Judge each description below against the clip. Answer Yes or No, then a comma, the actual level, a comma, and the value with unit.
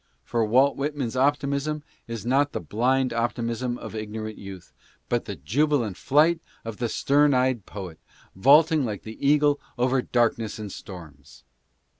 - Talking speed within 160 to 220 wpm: No, average, 145 wpm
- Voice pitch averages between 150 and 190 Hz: No, low, 120 Hz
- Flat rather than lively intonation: No, average, 4.6 semitones